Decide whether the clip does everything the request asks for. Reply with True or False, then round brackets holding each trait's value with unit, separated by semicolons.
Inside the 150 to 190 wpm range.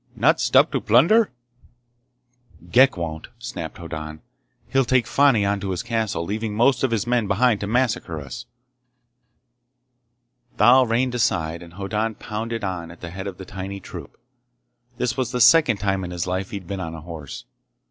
True (170 wpm)